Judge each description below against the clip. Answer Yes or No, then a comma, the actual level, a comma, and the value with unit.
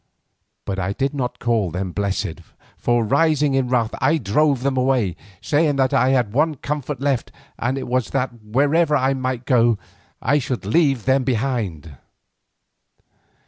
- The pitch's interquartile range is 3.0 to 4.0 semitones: Yes, average, 3.5 semitones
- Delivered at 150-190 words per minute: Yes, average, 160 wpm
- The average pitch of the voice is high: No, low, 130 Hz